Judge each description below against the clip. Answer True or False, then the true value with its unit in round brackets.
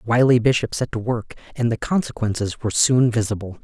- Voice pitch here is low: True (115 Hz)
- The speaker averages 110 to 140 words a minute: False (200 wpm)